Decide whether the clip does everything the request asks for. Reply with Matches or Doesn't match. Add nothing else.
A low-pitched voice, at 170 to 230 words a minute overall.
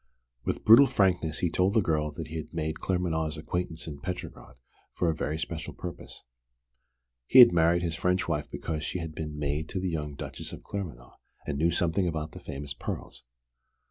Matches